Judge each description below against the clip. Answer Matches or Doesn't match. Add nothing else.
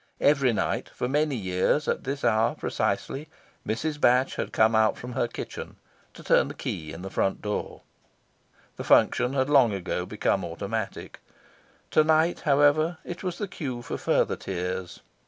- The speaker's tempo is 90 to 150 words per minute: Doesn't match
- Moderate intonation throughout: Doesn't match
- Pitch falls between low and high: Doesn't match